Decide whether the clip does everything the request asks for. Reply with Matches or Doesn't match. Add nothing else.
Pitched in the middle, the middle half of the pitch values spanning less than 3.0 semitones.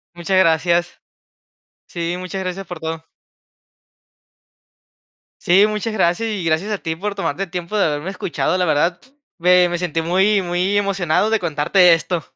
Matches